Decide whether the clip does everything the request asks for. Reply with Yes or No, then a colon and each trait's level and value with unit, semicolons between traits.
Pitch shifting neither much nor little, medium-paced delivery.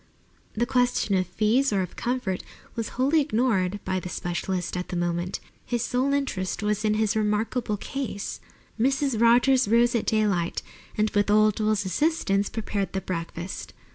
Yes: average, 4.3 semitones; average, 160 wpm